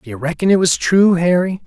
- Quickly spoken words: Yes, fast, 255 wpm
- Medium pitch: Yes, medium, 170 Hz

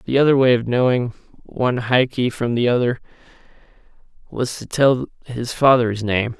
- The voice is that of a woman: No, male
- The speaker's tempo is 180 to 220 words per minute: No, average, 150 wpm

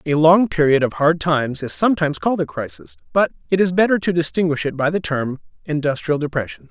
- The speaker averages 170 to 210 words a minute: Yes, fast, 205 wpm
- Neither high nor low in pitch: Yes, medium, 155 Hz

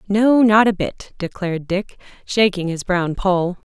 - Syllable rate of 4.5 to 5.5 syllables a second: No, 4.2 syllables/s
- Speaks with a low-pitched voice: No, high, 190 Hz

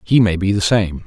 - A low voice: Yes, very low, 95 Hz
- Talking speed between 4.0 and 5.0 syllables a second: No, 5.3 syllables/s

